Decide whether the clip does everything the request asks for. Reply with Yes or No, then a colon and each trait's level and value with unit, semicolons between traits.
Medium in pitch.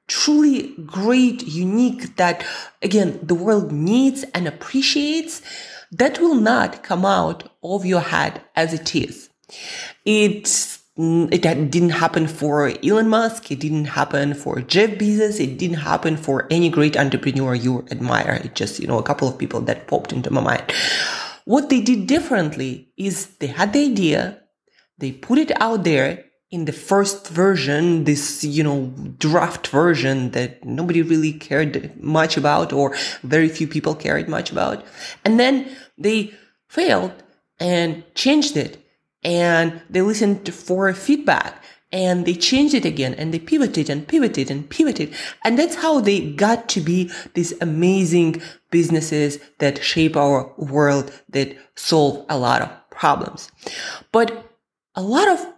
Yes: medium, 175 Hz